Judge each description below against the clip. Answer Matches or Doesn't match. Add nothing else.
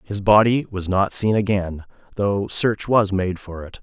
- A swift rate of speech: Doesn't match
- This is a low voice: Matches